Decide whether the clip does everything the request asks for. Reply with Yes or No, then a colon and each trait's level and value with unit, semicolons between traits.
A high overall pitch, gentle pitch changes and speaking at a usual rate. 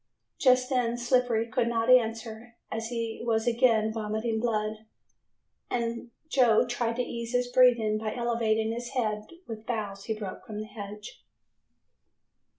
Yes: high, 230 Hz; narrow, 1.8 semitones; average, 145 wpm